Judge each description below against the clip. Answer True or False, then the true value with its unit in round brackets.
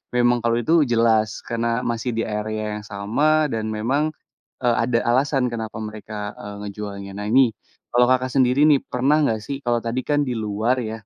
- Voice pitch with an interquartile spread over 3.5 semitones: False (3.1 semitones)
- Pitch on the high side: False (115 Hz)